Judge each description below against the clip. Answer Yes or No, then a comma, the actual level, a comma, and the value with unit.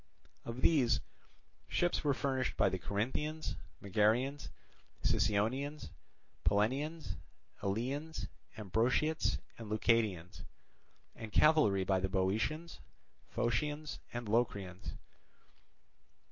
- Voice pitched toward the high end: No, low, 120 Hz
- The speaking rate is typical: No, slow, 85 wpm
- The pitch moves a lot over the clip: Yes, wide, 6.2 semitones